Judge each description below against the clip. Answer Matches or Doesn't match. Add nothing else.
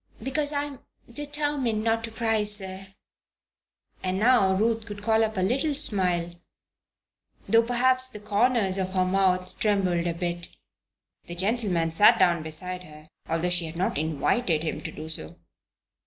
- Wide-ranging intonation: Doesn't match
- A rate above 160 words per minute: Doesn't match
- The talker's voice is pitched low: Doesn't match